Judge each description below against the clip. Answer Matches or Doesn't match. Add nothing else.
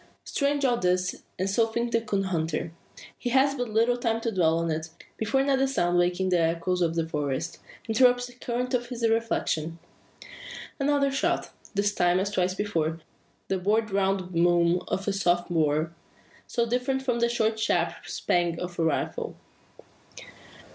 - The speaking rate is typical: Matches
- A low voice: Doesn't match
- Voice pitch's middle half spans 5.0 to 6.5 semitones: Matches